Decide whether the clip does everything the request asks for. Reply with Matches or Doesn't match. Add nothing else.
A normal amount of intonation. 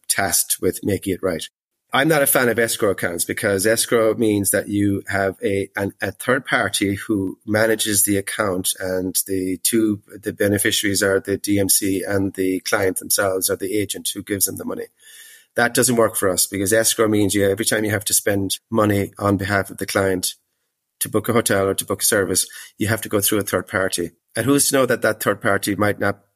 Doesn't match